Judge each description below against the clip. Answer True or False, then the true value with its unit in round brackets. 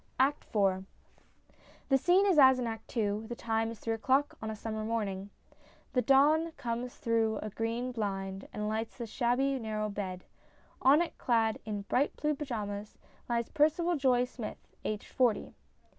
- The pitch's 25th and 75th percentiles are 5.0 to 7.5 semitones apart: False (3.8 semitones)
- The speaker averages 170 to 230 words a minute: True (175 wpm)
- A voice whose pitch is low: False (230 Hz)